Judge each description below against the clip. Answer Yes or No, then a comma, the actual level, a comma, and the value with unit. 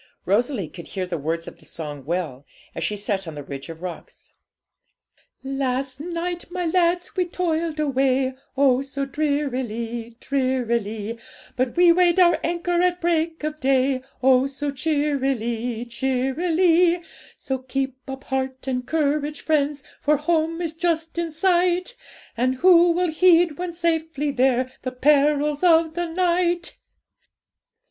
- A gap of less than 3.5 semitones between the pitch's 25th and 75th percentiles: No, average, 5.0 semitones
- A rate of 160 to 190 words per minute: No, average, 140 wpm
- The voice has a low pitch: No, very high, 285 Hz